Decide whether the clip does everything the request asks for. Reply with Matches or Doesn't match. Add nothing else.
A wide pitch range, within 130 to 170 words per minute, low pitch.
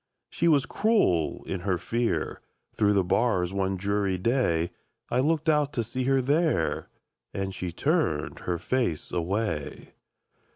Matches